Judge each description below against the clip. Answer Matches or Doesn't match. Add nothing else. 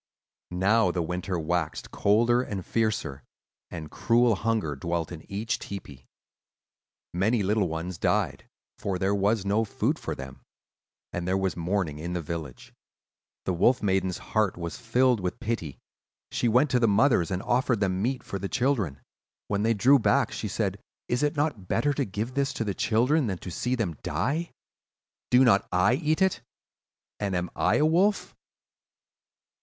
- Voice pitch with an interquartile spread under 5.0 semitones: Doesn't match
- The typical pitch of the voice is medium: Doesn't match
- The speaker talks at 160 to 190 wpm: Matches